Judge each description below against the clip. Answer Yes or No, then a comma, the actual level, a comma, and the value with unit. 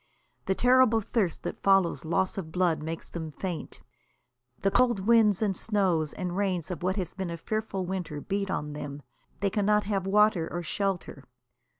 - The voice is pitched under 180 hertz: No, high, 190 Hz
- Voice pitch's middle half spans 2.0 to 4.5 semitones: Yes, average, 3.4 semitones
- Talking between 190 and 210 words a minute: No, average, 175 wpm